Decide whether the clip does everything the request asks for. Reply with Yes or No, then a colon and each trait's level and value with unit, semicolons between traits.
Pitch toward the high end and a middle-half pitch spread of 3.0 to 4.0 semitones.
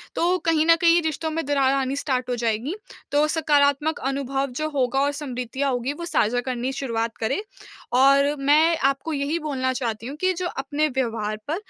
Yes: very high, 275 Hz; average, 3.4 semitones